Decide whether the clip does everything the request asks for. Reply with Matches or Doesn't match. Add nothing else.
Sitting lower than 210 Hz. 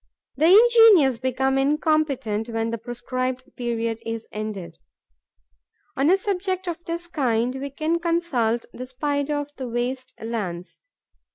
Doesn't match